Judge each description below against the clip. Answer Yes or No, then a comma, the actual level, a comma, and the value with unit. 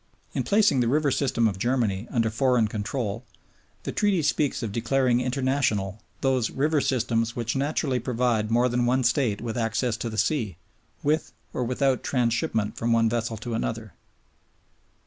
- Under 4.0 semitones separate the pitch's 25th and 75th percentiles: Yes, average, 2.8 semitones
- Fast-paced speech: No, average, 160 wpm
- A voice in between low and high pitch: No, low, 120 Hz